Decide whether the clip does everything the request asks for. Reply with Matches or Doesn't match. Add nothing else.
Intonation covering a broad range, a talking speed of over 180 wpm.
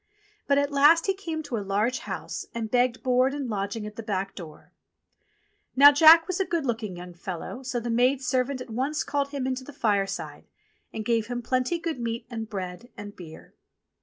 Doesn't match